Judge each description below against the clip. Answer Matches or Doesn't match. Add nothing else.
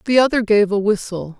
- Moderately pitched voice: Doesn't match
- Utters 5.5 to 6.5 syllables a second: Matches